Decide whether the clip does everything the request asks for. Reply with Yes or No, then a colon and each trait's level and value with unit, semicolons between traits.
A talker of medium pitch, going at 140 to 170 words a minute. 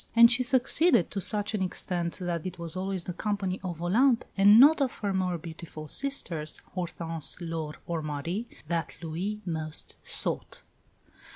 Yes: medium, 180 Hz; average, 160 wpm